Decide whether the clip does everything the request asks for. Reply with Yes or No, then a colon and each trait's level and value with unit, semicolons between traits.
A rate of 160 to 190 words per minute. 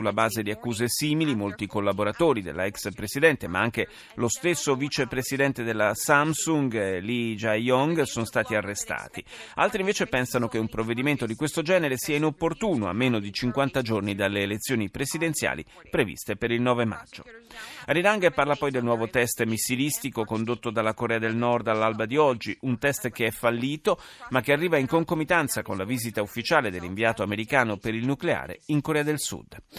Yes: fast, 170 wpm